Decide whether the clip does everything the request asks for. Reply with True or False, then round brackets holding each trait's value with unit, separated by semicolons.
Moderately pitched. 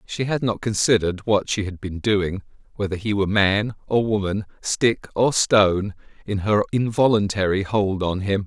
False (100 Hz)